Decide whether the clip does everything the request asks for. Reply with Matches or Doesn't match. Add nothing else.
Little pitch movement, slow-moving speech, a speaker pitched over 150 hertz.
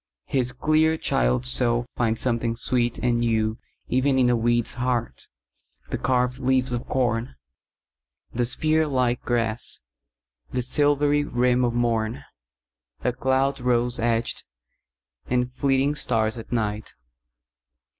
Doesn't match